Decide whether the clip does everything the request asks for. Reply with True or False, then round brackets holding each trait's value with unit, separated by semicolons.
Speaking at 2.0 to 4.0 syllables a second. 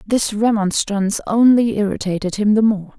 False (5.1 syllables/s)